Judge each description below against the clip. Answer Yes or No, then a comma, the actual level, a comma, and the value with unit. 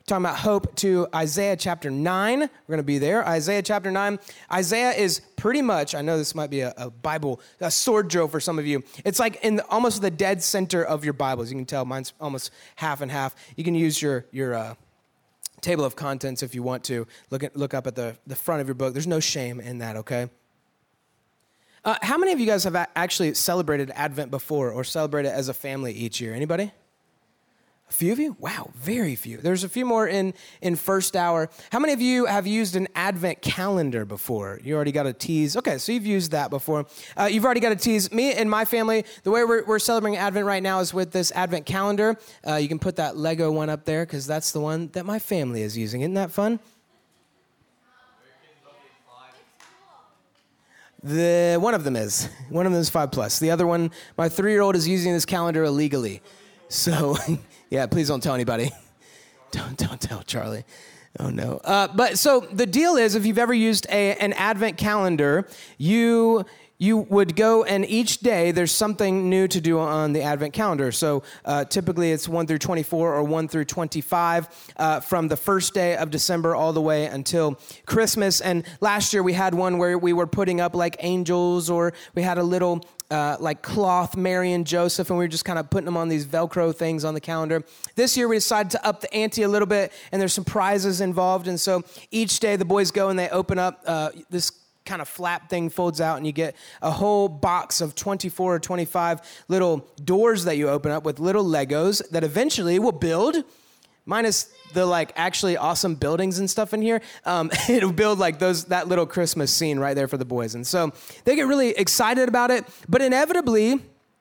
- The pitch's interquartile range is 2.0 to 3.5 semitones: No, average, 4.9 semitones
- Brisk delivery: Yes, fast, 210 wpm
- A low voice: No, medium, 175 Hz